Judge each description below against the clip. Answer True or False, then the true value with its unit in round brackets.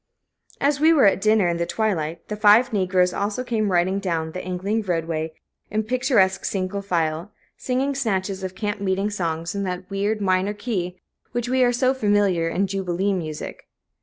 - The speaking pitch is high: True (195 Hz)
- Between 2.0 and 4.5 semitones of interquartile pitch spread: True (3.2 semitones)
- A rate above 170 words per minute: True (180 wpm)